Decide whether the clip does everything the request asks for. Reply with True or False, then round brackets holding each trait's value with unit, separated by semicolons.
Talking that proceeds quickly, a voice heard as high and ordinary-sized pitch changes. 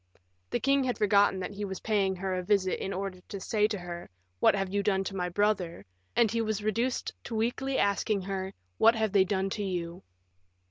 False (215 wpm; 200 Hz; 2.3 semitones)